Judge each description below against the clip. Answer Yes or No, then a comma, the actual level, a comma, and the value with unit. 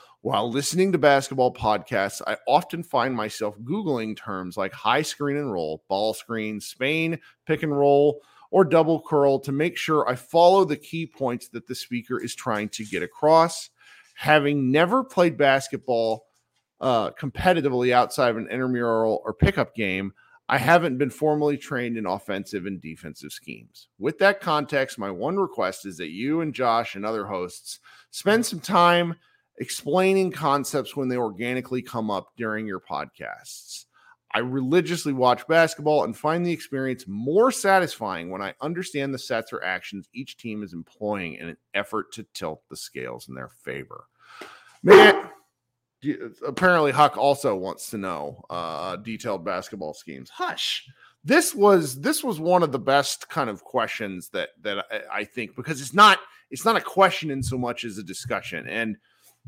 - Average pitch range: No, wide, 6.3 semitones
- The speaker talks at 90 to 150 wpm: No, average, 165 wpm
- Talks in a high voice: No, low, 135 Hz